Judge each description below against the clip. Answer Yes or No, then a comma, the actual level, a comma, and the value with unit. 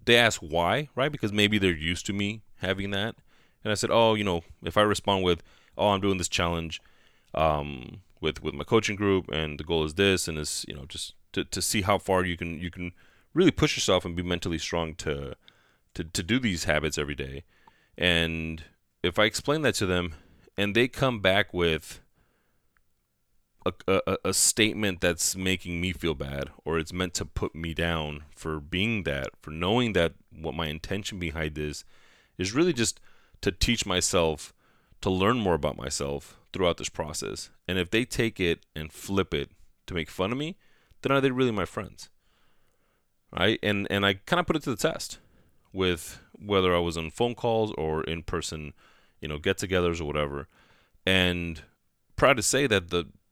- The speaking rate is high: No, average, 195 wpm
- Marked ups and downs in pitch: No, average, 4.3 semitones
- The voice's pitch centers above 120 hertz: No, very low, 90 Hz